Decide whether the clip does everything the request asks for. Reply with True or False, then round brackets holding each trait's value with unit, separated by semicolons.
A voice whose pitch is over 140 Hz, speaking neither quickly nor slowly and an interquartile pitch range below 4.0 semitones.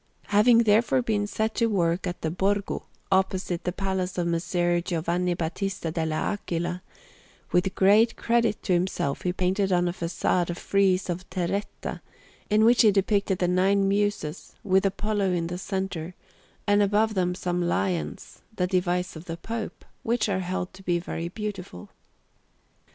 True (185 Hz; 160 wpm; 2.6 semitones)